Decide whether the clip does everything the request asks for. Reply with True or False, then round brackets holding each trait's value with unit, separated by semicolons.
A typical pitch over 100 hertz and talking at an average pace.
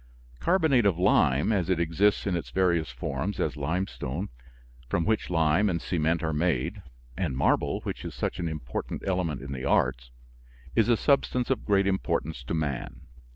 False (85 Hz; 170 wpm)